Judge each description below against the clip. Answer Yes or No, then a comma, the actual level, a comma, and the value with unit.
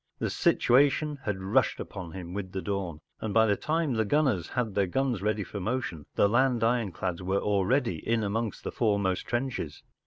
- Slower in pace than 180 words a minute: No, average, 185 wpm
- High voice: No, low, 105 Hz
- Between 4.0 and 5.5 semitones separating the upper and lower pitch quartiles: Yes, average, 4.3 semitones